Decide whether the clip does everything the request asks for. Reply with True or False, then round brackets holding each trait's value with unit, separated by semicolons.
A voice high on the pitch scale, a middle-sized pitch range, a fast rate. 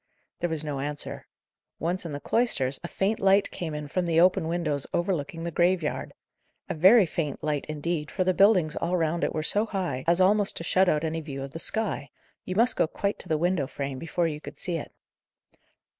False (170 Hz; 3.7 semitones; 215 wpm)